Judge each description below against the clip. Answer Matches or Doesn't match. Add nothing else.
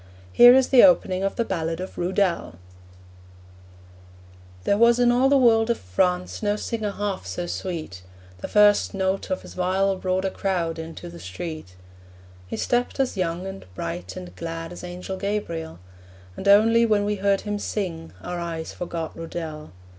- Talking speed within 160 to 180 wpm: Matches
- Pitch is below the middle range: Doesn't match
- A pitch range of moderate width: Matches